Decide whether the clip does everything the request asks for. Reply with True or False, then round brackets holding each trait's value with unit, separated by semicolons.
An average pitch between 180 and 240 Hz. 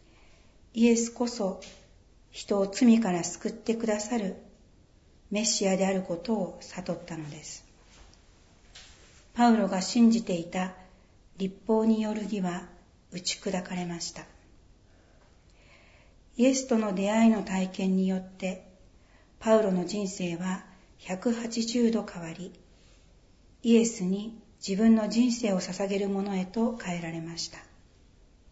True (190 Hz)